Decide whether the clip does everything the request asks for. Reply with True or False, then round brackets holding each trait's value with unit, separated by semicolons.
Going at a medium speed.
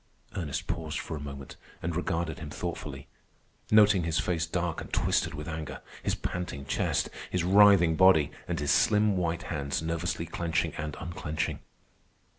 True (155 wpm)